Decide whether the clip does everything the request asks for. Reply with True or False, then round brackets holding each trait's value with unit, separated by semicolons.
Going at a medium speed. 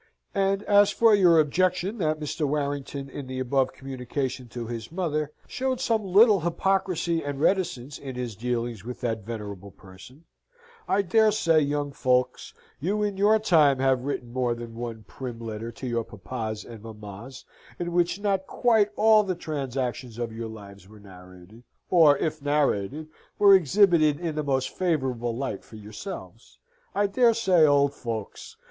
True (165 wpm)